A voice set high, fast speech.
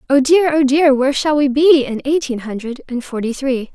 Yes: very high, 275 Hz; fast, 225 wpm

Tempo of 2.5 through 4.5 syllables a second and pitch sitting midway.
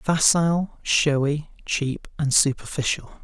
Yes: 3.8 syllables/s; medium, 150 Hz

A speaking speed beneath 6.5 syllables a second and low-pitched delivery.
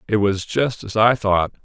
Yes: 4.4 syllables/s; low, 110 Hz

